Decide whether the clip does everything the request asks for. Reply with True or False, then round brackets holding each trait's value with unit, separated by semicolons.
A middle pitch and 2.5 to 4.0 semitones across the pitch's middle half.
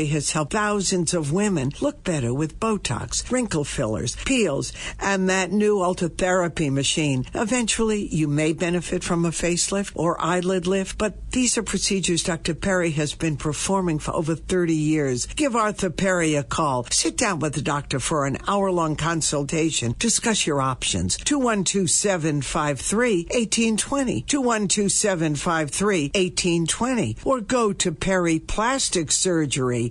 False (175 Hz; 4.8 semitones)